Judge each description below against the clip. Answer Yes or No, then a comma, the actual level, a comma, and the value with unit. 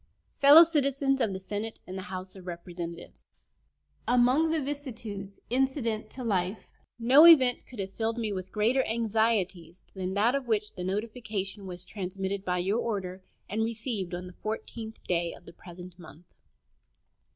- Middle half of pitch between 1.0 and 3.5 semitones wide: No, average, 4.5 semitones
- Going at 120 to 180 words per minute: Yes, average, 165 wpm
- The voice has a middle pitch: No, high, 210 Hz